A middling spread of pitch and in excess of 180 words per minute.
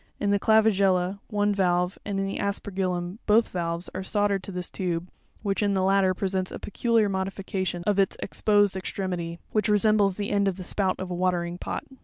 No: narrow, 2.0 semitones; average, 195 wpm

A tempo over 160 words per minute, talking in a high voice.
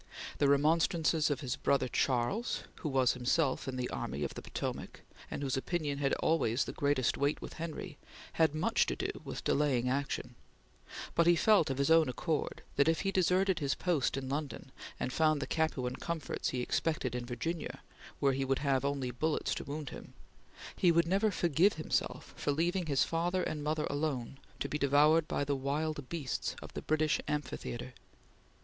No: average, 185 wpm; medium, 145 Hz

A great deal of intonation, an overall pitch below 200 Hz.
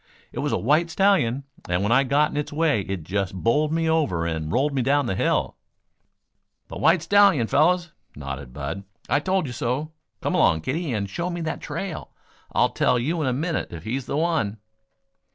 Yes: wide, 8.1 semitones; medium, 140 Hz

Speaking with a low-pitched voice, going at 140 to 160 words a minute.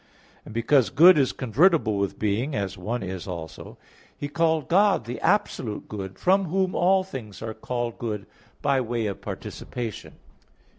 Yes: low, 120 Hz; average, 155 wpm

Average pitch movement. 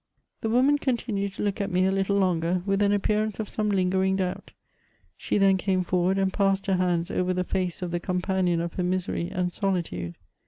No: narrow, 1.8 semitones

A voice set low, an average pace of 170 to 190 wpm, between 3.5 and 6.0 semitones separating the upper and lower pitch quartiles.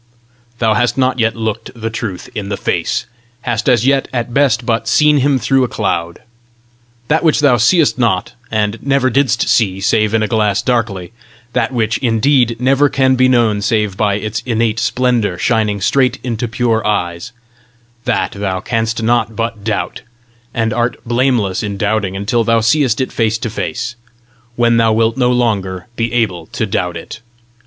No: low, 115 Hz; average, 175 wpm; average, 2.7 semitones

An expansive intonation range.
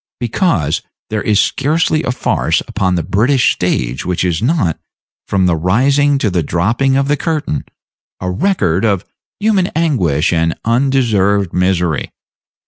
Yes: wide, 7.5 semitones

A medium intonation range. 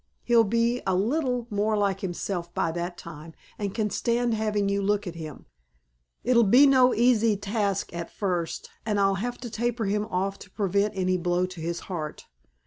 Yes: average, 3.9 semitones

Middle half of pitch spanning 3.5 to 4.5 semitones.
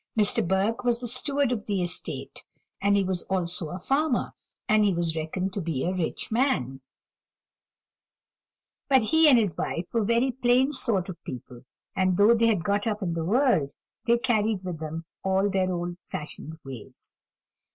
No: average, 5.2 semitones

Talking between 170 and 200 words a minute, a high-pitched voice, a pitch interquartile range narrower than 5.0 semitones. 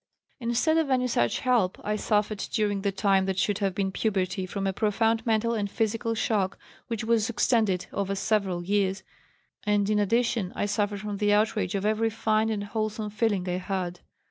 Yes: average, 185 wpm; high, 210 Hz; narrow, 2.4 semitones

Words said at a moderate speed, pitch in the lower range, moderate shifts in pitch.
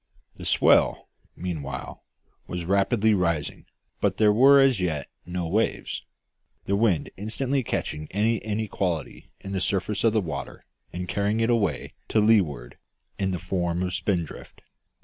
Yes: average, 145 wpm; very low, 95 Hz; average, 3.9 semitones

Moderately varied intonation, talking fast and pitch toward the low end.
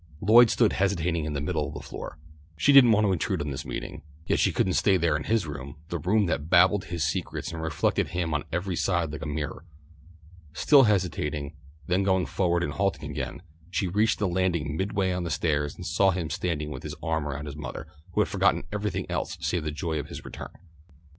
Yes: average, 4.0 semitones; fast, 220 wpm; very low, 85 Hz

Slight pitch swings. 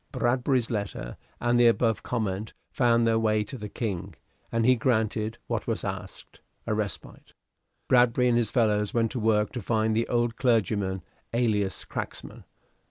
Yes: narrow, 2.2 semitones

